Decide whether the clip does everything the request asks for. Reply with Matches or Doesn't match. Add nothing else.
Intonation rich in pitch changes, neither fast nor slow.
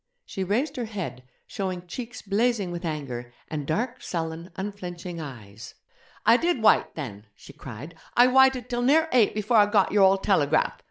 Matches